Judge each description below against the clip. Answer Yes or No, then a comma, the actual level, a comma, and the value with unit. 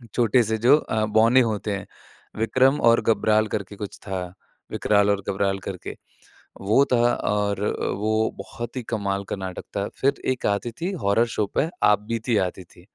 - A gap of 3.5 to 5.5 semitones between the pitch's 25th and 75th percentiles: No, average, 2.8 semitones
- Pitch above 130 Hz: No, low, 105 Hz